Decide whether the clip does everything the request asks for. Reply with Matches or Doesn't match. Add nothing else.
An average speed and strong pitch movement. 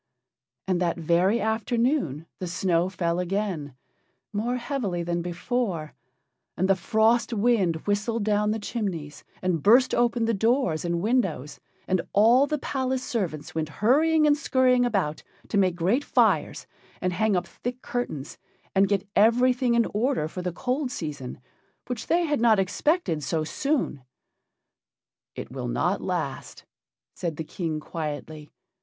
Matches